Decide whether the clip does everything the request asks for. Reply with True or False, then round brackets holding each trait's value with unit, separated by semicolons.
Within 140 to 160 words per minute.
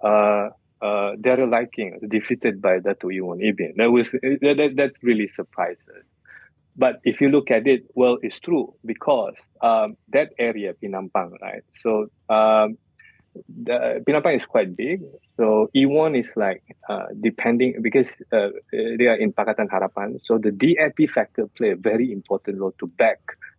True (150 wpm)